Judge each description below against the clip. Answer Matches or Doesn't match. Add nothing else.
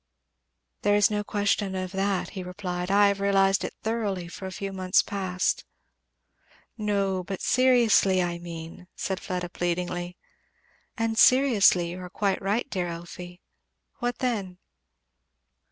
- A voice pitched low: Doesn't match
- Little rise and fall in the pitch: Matches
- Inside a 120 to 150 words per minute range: Matches